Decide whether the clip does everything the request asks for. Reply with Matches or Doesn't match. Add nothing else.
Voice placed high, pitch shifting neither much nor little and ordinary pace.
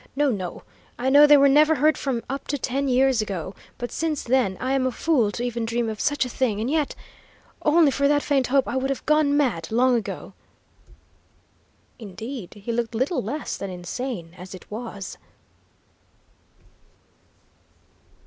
Matches